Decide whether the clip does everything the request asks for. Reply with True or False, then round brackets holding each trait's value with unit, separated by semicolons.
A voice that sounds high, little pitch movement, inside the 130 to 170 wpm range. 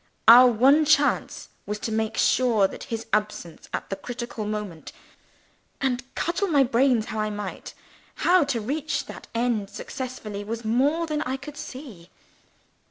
False (240 Hz; 4.5 semitones; 155 wpm)